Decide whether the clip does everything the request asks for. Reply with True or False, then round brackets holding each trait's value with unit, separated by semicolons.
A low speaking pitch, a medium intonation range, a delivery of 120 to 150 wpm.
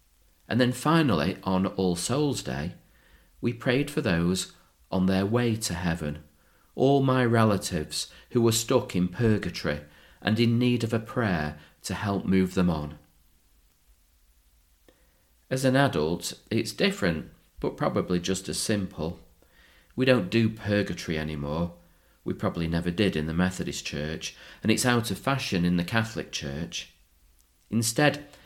False (90 Hz; 6.5 semitones; 145 wpm)